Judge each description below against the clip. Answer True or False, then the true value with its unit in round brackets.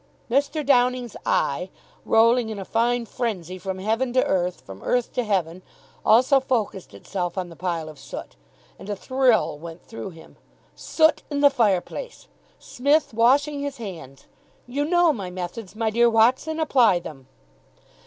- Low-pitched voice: False (230 Hz)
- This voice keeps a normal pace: True (155 wpm)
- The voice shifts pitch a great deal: True (6.0 semitones)